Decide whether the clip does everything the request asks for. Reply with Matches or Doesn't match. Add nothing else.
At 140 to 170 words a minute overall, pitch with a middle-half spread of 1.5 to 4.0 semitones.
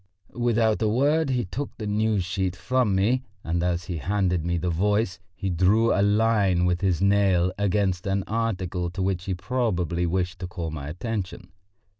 Doesn't match